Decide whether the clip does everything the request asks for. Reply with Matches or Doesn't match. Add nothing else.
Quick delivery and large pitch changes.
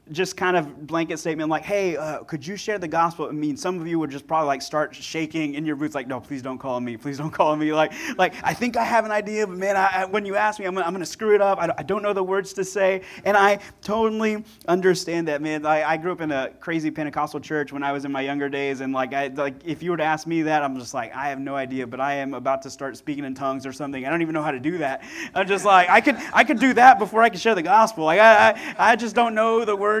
Matches